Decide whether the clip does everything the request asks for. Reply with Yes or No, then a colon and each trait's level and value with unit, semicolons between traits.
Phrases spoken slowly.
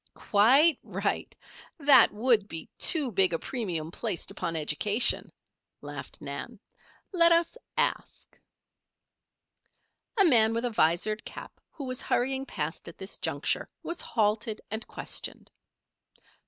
Yes: slow, 125 wpm